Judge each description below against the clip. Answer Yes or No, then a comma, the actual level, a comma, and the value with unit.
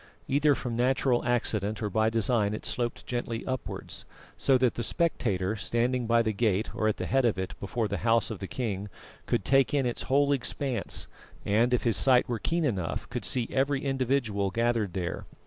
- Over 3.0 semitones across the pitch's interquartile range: Yes, average, 3.6 semitones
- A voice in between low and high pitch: No, low, 120 Hz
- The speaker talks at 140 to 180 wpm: No, average, 195 wpm